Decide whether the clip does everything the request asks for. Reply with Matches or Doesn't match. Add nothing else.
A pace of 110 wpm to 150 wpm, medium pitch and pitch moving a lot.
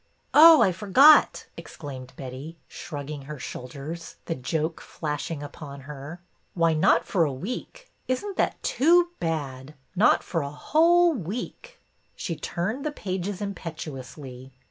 Matches